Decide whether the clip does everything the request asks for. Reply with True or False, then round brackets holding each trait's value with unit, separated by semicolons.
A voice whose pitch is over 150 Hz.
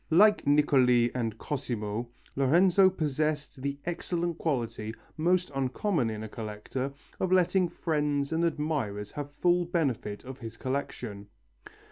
False (140 Hz)